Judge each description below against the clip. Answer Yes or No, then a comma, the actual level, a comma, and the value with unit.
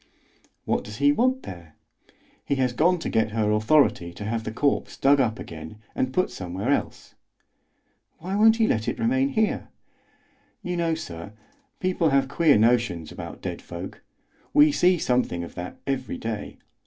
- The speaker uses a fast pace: No, average, 165 wpm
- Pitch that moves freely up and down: Yes, wide, 8.0 semitones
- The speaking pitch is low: Yes, low, 130 Hz